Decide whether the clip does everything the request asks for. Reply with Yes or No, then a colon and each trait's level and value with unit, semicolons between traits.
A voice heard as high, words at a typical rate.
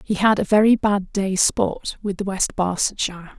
Yes: high, 200 Hz; average, 195 wpm